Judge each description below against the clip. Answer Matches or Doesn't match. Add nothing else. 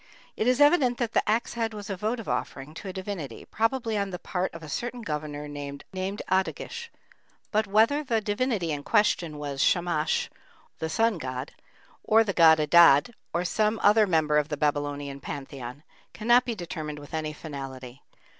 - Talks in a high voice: Doesn't match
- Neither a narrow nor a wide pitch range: Doesn't match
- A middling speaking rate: Matches